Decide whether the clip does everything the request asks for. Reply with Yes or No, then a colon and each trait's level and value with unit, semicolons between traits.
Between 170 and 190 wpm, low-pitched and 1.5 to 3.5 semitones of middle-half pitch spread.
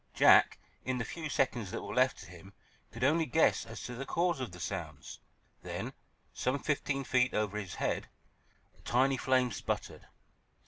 No: average, 175 wpm; low, 125 Hz; average, 4.7 semitones